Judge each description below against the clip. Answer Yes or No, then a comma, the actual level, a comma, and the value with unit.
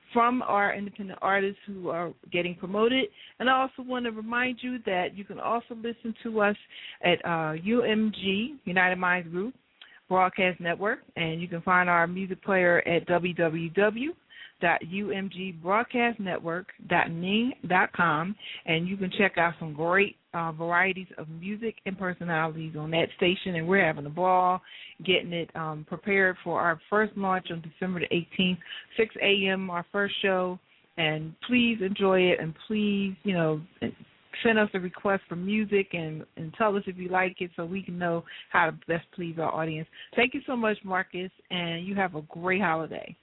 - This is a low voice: No, medium, 185 Hz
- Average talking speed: Yes, average, 175 wpm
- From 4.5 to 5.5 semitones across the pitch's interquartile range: No, average, 3.2 semitones